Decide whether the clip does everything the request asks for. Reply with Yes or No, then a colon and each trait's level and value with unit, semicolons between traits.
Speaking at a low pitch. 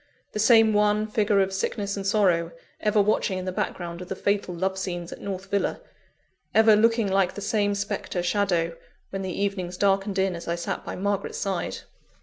No: high, 195 Hz